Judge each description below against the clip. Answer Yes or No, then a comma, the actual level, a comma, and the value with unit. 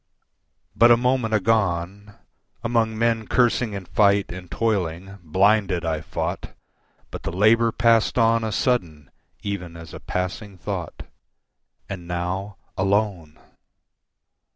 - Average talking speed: No, slow, 120 wpm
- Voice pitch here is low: Yes, low, 100 Hz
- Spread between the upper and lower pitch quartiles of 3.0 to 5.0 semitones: Yes, average, 4.1 semitones